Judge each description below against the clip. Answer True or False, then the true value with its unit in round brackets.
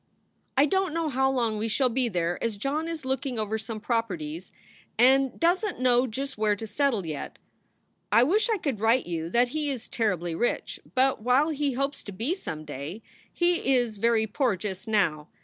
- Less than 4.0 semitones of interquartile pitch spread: False (4.8 semitones)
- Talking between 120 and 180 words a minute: False (190 wpm)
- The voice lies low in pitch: False (240 Hz)